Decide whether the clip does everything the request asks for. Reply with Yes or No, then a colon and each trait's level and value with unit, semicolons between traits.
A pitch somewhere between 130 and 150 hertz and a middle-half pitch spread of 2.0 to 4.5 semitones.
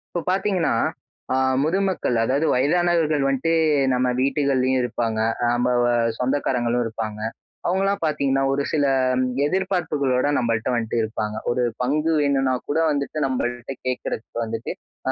Yes: low, 135 Hz; average, 4.1 semitones